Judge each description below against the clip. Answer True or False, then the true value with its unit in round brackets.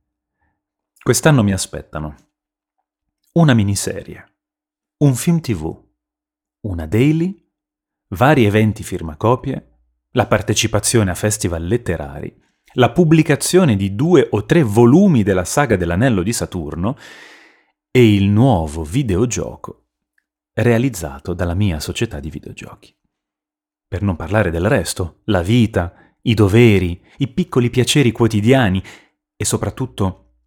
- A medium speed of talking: False (110 wpm)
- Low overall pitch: True (105 Hz)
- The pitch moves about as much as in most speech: False (6.0 semitones)